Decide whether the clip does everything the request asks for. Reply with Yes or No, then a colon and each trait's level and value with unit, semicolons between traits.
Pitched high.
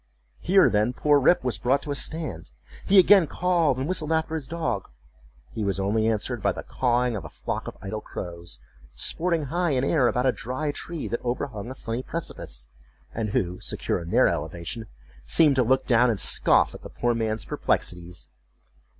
No: low, 125 Hz